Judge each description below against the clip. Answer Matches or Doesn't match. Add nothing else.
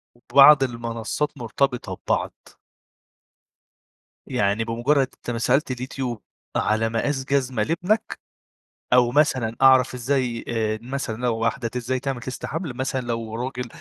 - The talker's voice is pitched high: Doesn't match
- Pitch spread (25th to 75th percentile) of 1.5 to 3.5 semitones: Matches